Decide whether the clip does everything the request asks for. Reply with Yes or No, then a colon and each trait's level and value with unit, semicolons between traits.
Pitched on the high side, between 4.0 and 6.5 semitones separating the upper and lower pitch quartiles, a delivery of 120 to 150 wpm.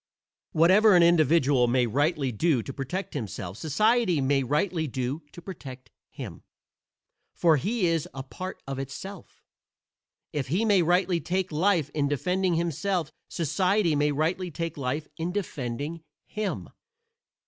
No: medium, 160 Hz; average, 4.9 semitones; slow, 135 wpm